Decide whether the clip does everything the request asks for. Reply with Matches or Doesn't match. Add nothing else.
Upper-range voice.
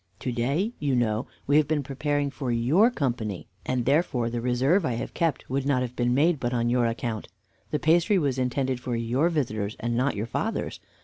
Doesn't match